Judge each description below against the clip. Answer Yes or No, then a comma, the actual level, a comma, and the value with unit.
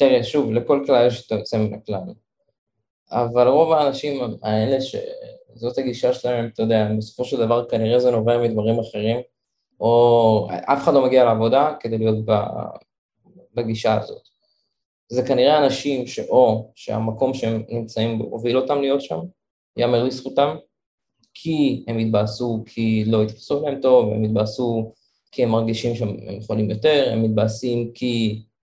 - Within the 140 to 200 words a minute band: Yes, average, 145 wpm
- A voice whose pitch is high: No, low, 120 Hz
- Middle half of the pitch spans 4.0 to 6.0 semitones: No, average, 3.2 semitones